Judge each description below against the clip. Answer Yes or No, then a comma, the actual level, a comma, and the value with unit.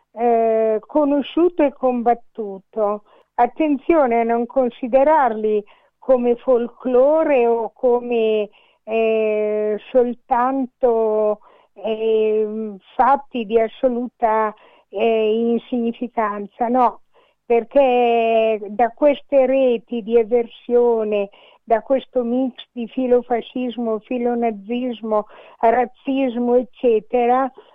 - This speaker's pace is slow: Yes, slow, 75 wpm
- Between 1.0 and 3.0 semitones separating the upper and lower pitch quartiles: Yes, narrow, 2.4 semitones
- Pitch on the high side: Yes, high, 240 Hz